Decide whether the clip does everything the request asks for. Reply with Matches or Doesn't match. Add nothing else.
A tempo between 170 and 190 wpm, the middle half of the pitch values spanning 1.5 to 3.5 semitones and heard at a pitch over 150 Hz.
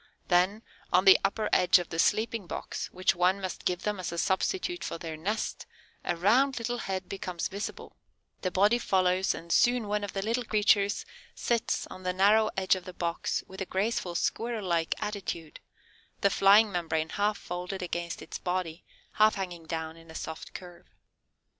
Matches